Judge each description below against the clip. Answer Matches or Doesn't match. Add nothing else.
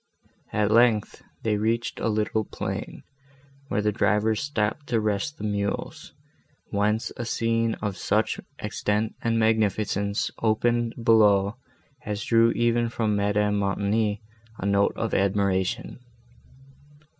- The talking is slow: Matches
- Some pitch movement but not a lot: Doesn't match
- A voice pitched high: Doesn't match